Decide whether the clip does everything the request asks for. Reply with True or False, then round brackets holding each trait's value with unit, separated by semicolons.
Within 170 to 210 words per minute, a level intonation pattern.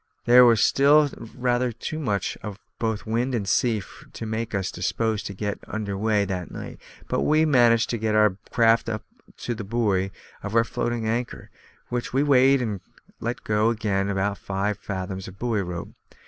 False (180 wpm; 3.1 semitones)